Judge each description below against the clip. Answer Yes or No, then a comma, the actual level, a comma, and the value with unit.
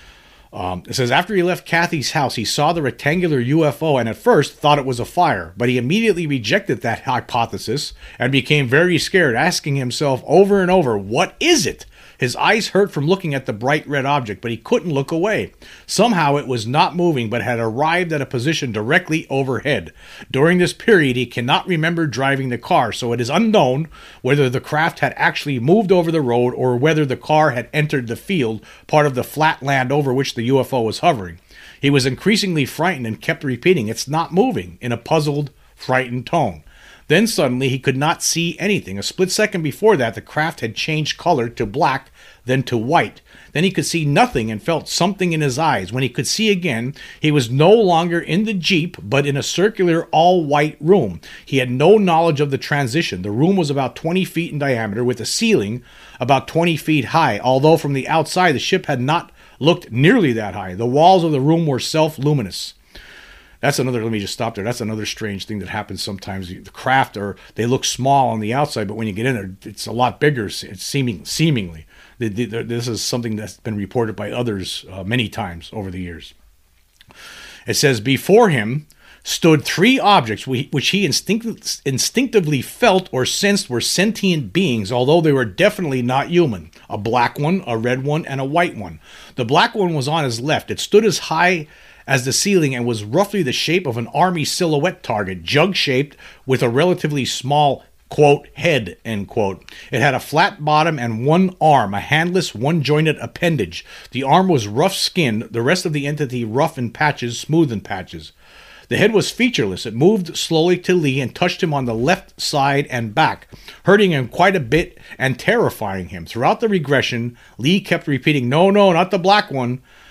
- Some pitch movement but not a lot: No, wide, 6.0 semitones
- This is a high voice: No, medium, 140 Hz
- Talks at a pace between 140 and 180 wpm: No, average, 200 wpm